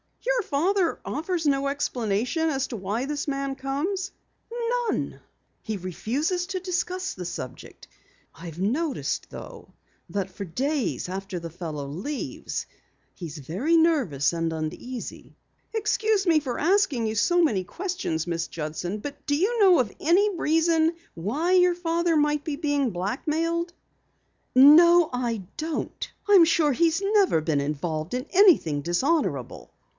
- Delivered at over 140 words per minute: No, slow, 135 wpm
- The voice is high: Yes, very high, 285 Hz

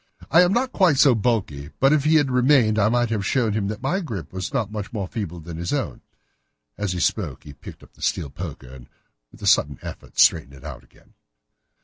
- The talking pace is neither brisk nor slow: No, fast, 230 wpm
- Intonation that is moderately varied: No, wide, 8.1 semitones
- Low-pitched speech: Yes, low, 105 Hz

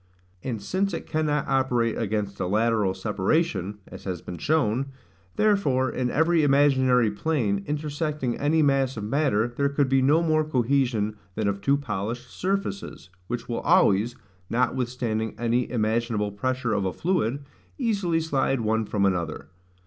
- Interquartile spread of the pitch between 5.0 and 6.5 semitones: Yes, wide, 5.4 semitones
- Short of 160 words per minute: Yes, average, 150 wpm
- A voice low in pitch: Yes, low, 125 Hz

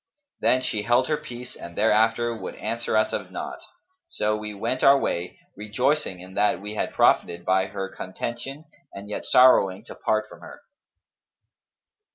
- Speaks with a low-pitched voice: Yes, low, 110 Hz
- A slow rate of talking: No, average, 165 wpm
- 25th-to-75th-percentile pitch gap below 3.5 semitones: No, average, 4.0 semitones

